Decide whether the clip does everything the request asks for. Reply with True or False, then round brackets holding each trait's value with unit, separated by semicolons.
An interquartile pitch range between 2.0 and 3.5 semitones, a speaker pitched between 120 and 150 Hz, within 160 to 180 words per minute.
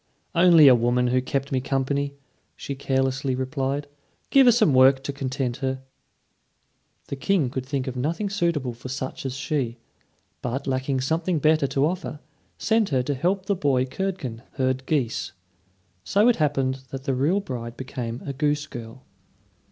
True (2.8 semitones; 135 Hz; 165 wpm)